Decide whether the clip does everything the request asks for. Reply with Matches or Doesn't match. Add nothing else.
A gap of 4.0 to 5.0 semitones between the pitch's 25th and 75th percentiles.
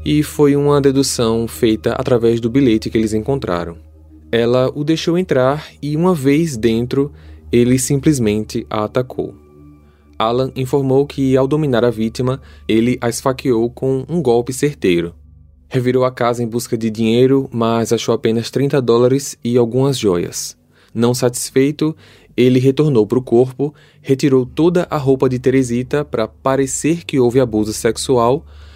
Doesn't match